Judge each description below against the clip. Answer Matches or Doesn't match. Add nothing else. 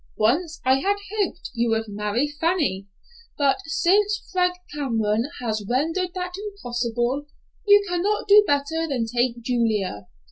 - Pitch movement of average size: Doesn't match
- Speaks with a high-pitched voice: Matches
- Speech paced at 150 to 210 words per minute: Doesn't match